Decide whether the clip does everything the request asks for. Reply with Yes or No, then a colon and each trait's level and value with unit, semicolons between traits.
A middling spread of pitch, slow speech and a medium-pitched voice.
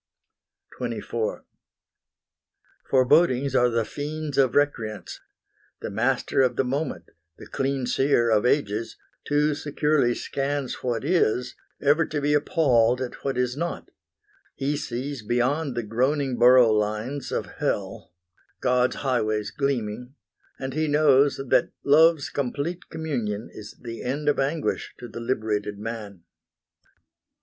No: average, 3.7 semitones; slow, 125 wpm; low, 130 Hz